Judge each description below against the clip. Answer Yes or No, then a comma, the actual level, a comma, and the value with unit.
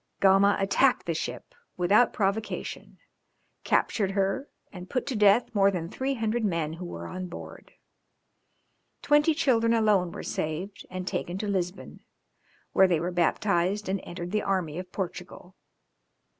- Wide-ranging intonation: No, average, 3.1 semitones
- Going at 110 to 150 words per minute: Yes, average, 145 wpm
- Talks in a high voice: Yes, high, 195 Hz